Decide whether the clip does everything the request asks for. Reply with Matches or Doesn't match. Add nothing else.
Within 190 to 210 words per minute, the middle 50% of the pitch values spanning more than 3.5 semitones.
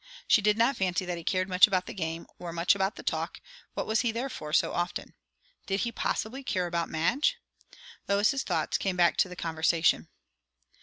Matches